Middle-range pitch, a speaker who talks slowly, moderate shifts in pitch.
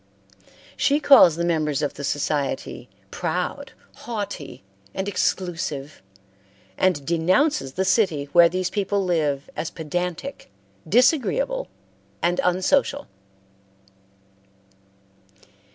Yes: medium, 180 Hz; slow, 90 wpm; average, 4.9 semitones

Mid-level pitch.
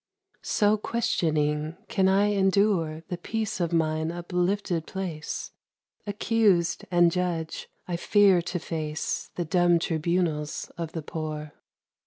Yes: medium, 175 Hz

